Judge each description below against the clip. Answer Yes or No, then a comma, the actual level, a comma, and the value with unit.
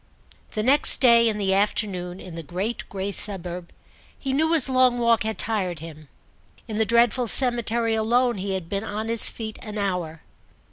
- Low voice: No, high, 215 Hz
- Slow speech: No, average, 180 wpm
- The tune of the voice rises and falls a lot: No, average, 3.8 semitones